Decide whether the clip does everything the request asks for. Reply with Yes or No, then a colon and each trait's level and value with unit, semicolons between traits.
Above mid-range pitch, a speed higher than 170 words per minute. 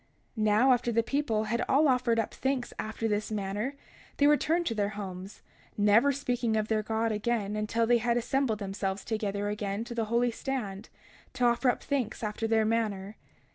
Yes: high, 225 Hz; average, 185 wpm